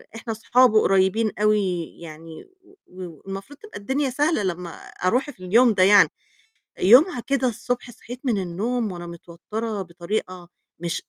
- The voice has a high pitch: Yes, high, 210 Hz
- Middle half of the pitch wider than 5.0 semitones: Yes, wide, 5.4 semitones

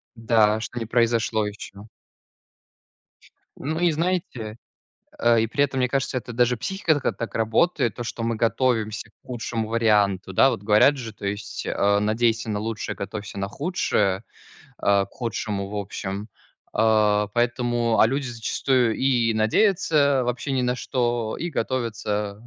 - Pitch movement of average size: Yes, average, 3.0 semitones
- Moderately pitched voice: No, low, 115 Hz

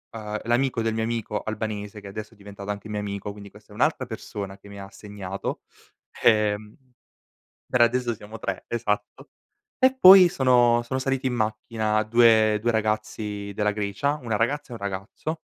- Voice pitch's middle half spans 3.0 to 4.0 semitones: No, narrow, 2.4 semitones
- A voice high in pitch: No, low, 110 Hz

